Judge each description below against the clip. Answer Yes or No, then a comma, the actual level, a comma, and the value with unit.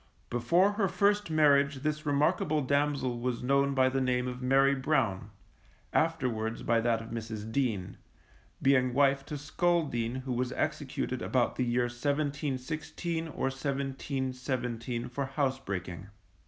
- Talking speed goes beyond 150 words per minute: No, slow, 135 wpm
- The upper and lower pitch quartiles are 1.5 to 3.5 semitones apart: Yes, average, 3.1 semitones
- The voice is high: No, low, 135 Hz